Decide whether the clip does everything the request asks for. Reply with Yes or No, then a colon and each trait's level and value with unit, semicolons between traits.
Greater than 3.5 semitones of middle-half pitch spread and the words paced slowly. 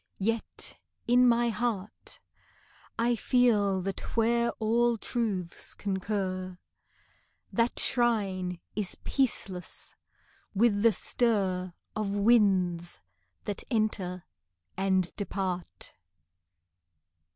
Yes: average, 3.9 semitones; slow, 85 wpm